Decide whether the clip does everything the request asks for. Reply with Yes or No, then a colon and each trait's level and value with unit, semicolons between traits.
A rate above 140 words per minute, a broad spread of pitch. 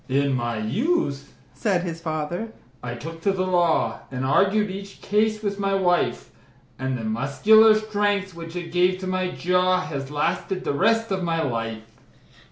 Yes: average, 170 wpm; wide, 6.1 semitones